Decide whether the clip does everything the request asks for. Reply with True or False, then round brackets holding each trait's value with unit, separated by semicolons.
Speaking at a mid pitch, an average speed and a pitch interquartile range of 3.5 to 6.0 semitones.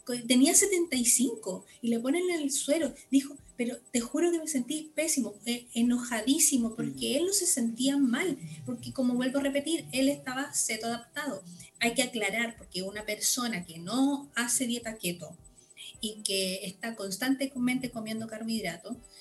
False (245 Hz; 155 wpm; 3.8 semitones)